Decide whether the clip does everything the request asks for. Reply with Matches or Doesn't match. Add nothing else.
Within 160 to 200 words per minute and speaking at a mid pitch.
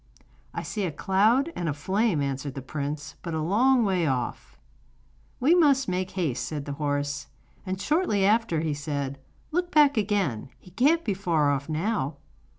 Matches